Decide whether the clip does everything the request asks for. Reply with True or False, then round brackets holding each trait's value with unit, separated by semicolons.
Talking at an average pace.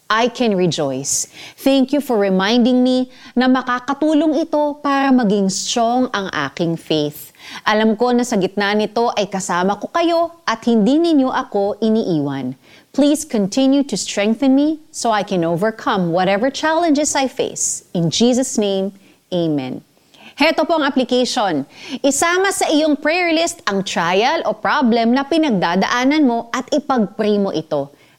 True (145 wpm)